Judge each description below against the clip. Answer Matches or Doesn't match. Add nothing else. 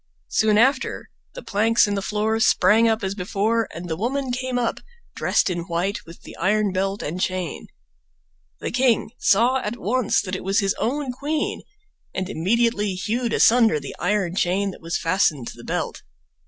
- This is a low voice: Doesn't match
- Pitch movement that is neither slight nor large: Matches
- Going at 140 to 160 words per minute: Doesn't match